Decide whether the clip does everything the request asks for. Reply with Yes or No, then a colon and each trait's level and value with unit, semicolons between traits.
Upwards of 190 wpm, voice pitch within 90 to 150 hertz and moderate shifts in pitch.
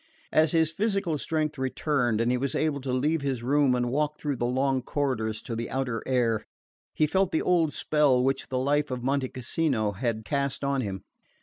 Yes: average, 200 wpm; low, 135 Hz; average, 3.4 semitones